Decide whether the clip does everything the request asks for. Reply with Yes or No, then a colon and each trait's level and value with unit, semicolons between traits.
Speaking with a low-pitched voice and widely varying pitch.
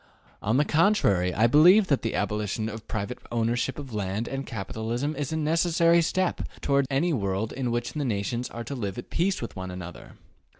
Yes: low, 120 Hz; wide, 5.9 semitones